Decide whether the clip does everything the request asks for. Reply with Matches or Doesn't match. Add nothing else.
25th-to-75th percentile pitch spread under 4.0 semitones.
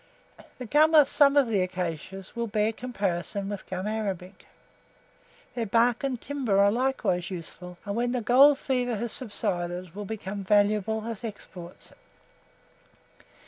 Doesn't match